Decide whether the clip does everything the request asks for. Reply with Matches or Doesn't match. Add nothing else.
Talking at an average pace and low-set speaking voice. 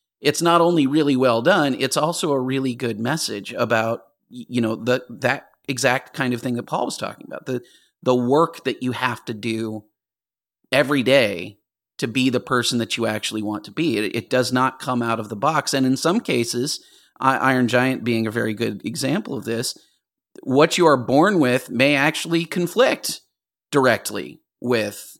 Matches